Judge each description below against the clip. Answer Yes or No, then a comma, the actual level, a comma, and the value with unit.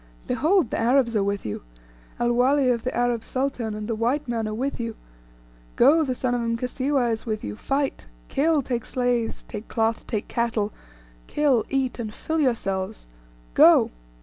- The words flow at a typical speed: Yes, average, 175 wpm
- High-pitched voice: Yes, high, 240 Hz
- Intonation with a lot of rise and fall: No, average, 3.2 semitones